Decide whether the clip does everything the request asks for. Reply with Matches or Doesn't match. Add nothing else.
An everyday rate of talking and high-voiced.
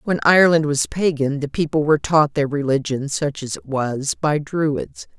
Doesn't match